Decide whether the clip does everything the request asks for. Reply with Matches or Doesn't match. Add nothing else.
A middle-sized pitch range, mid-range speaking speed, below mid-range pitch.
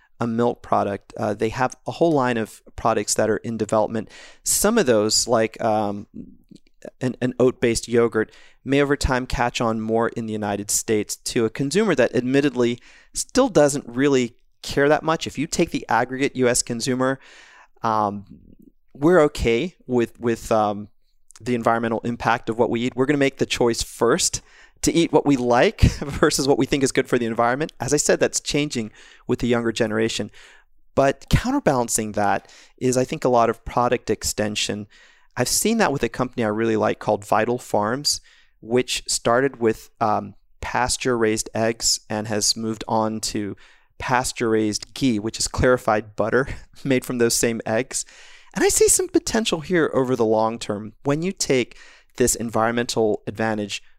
Matches